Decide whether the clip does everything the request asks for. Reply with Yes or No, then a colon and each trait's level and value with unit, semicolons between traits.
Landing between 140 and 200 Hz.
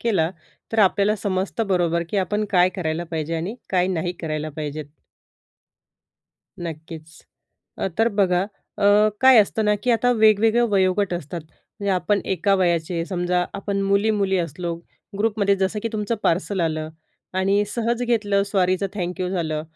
Yes: high, 190 Hz